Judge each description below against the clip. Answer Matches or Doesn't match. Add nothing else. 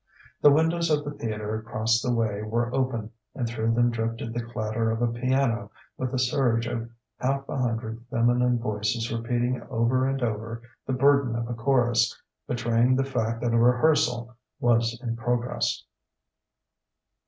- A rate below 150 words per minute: Doesn't match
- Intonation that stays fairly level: Matches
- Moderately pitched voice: Doesn't match